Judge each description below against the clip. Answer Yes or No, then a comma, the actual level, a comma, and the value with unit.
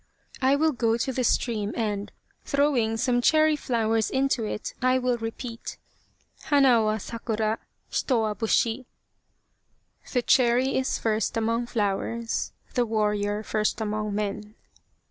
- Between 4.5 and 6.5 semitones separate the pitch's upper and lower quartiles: No, average, 2.8 semitones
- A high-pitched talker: Yes, high, 230 Hz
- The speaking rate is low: Yes, slow, 130 wpm